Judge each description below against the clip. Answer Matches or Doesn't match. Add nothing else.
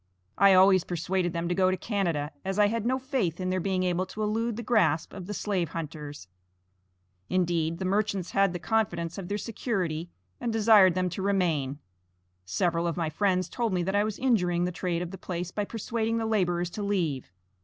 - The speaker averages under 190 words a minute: Doesn't match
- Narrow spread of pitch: Doesn't match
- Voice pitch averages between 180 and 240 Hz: Matches